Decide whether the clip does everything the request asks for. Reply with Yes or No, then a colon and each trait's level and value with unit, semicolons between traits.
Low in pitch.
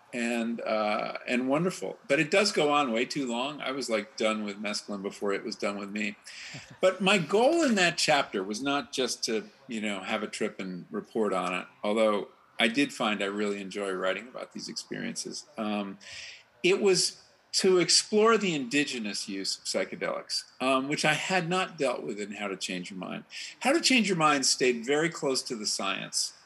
Yes: low, 130 Hz